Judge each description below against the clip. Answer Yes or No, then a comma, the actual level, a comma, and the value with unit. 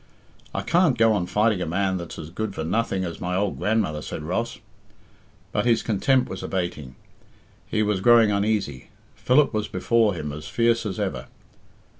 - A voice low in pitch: Yes, low, 100 Hz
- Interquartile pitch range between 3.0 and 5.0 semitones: Yes, average, 4.6 semitones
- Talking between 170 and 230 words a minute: Yes, average, 175 wpm